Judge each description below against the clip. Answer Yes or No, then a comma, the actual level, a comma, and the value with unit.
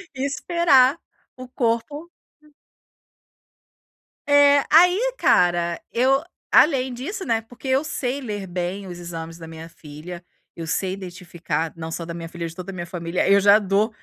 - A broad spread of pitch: Yes, wide, 7.6 semitones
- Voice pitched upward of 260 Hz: No, high, 200 Hz